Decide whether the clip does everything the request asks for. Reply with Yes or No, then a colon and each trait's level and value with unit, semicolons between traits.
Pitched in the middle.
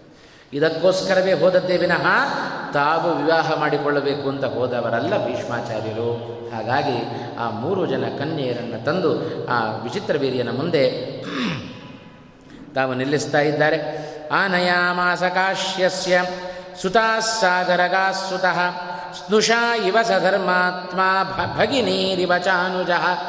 Yes: medium, 180 Hz